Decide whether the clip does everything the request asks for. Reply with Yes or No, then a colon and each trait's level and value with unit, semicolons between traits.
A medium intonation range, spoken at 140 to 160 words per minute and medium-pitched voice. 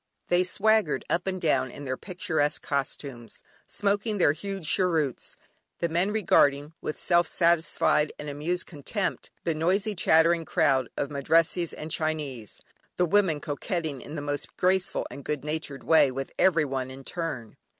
Yes: average, 3.9 semitones; average, 150 wpm; medium, 160 Hz